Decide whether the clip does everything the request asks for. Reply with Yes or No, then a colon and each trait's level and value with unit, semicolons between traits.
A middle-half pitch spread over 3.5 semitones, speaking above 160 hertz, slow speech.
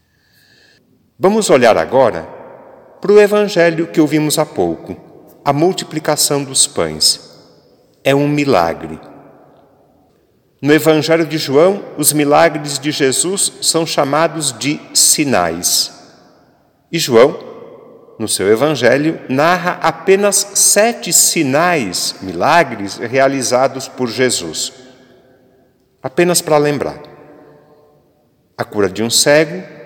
No: average, 4.4 semitones; medium, 150 Hz; slow, 100 wpm